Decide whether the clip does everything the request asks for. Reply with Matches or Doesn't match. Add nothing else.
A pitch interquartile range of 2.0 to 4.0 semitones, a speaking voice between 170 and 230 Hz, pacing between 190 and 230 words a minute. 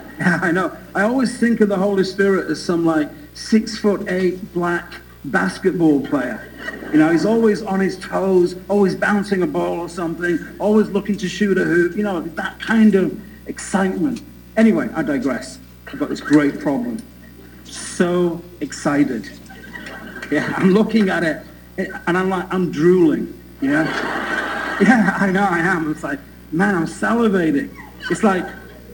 Doesn't match